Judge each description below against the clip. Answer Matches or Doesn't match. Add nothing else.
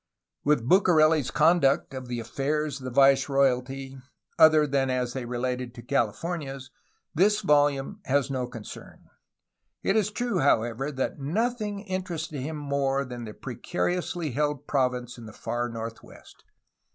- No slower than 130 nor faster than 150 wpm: Matches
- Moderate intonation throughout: Matches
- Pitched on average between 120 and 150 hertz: Matches